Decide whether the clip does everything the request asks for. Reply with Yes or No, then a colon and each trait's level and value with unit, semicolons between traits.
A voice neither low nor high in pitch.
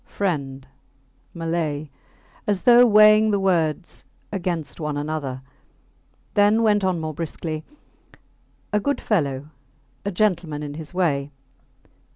Yes: medium, 170 Hz